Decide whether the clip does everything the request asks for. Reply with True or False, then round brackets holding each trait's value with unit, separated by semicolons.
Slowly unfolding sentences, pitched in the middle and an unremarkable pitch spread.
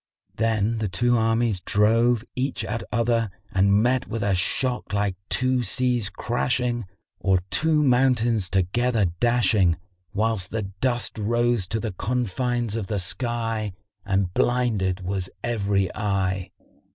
False (130 wpm; 115 Hz; 3.6 semitones)